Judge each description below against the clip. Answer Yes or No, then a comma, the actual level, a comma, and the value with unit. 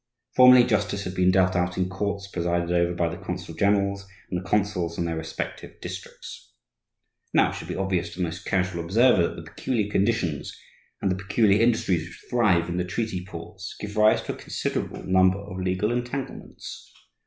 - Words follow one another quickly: No, average, 190 wpm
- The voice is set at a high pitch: No, very low, 95 Hz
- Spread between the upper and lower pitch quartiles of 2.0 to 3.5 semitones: Yes, average, 2.8 semitones